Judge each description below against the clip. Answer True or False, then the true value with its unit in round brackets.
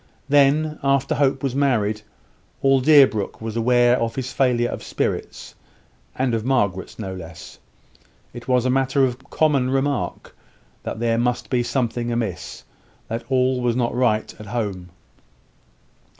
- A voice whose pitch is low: True (125 Hz)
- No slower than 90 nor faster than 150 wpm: True (145 wpm)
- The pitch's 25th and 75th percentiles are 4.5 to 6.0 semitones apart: False (2.7 semitones)